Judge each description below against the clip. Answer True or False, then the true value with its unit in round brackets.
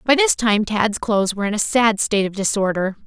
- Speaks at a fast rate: True (235 wpm)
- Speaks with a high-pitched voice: True (215 Hz)